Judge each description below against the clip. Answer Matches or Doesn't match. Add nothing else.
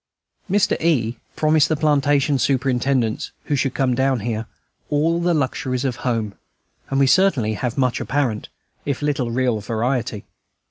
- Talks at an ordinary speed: Matches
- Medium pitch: Doesn't match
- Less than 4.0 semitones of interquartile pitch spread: Matches